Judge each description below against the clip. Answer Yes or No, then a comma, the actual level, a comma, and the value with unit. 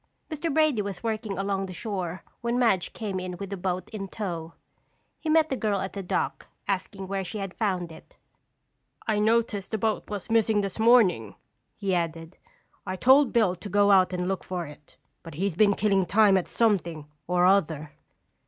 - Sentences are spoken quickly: No, average, 190 wpm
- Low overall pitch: No, high, 195 Hz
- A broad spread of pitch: No, average, 3.3 semitones